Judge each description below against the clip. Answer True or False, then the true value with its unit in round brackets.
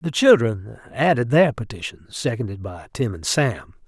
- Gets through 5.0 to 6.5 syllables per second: False (4.5 syllables/s)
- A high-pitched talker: False (120 Hz)